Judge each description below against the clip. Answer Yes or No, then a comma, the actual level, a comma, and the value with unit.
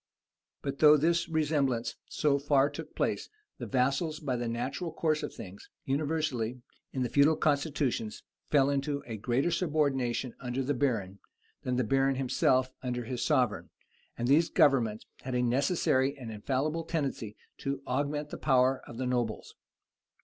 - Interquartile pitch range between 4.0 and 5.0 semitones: No, average, 3.1 semitones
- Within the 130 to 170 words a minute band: Yes, average, 155 wpm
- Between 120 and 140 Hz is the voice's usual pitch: Yes, low, 135 Hz